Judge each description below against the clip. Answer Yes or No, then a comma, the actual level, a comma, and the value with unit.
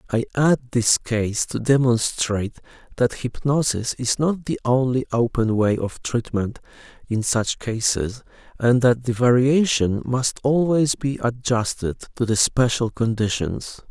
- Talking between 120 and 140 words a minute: Yes, slow, 135 wpm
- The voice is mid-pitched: No, low, 120 Hz